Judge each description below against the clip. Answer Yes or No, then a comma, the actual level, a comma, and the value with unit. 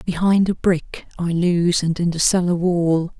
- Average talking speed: Yes, average, 170 wpm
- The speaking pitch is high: No, medium, 175 Hz